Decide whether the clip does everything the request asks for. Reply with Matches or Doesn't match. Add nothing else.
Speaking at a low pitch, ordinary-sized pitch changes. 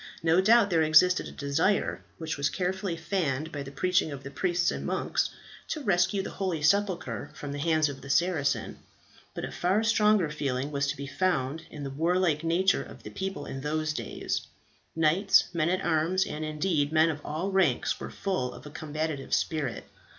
Doesn't match